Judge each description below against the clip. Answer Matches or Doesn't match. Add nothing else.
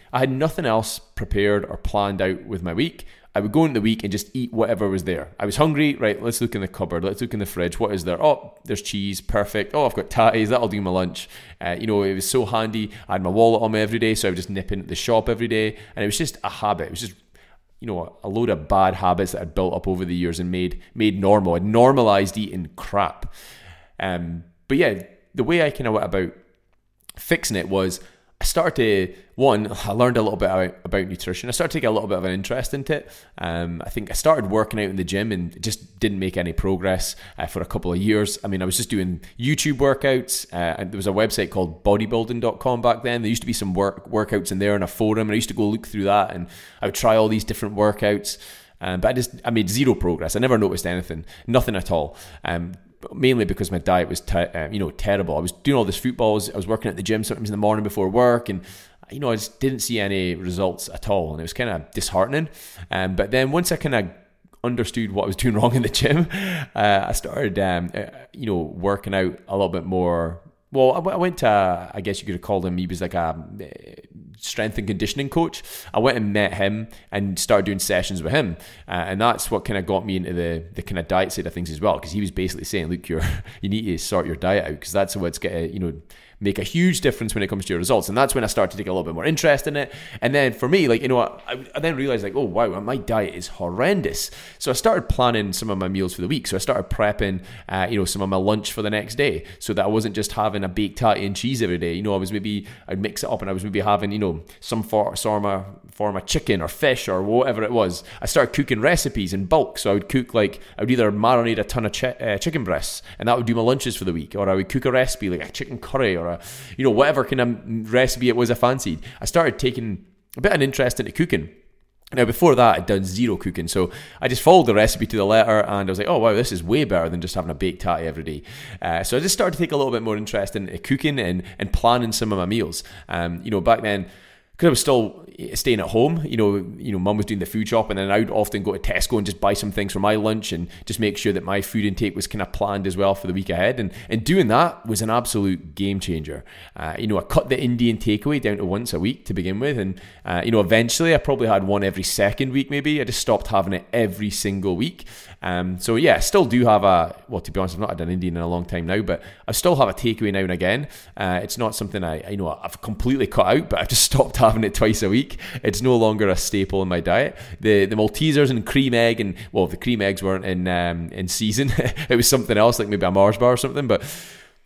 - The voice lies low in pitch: Matches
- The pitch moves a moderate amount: Matches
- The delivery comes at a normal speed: Doesn't match